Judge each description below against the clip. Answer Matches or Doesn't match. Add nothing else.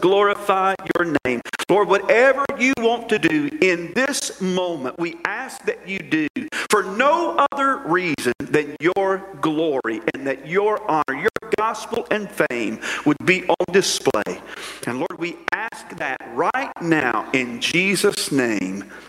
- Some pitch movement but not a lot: Doesn't match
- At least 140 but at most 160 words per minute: Matches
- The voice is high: Matches